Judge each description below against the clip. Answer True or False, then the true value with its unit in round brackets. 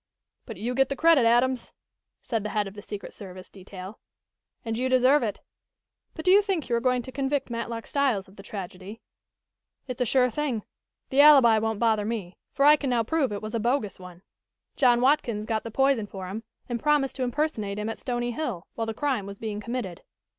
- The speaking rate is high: True (210 wpm)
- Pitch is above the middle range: True (235 Hz)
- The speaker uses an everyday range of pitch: True (4.2 semitones)